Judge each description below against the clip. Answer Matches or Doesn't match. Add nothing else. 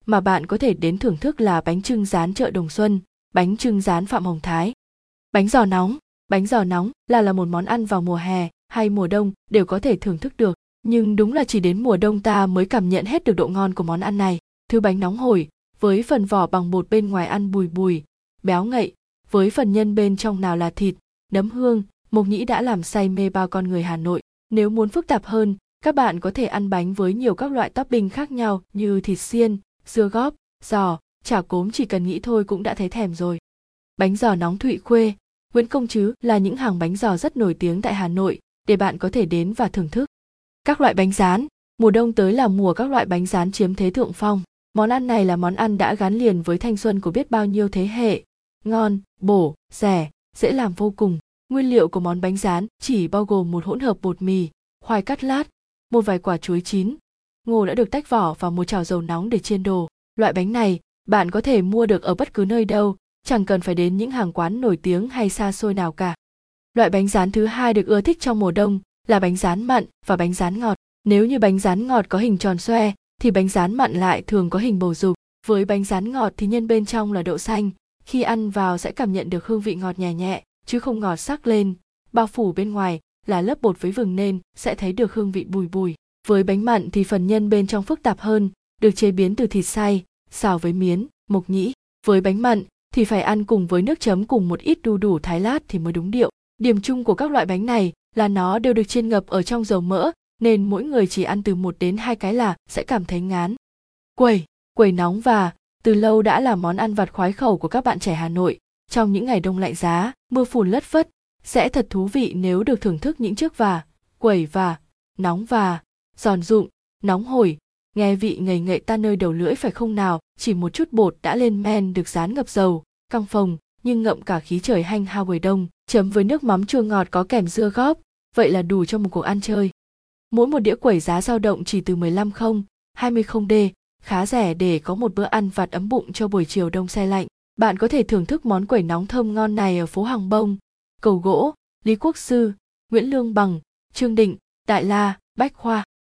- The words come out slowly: Doesn't match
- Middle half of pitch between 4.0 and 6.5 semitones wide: Doesn't match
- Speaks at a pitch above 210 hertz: Doesn't match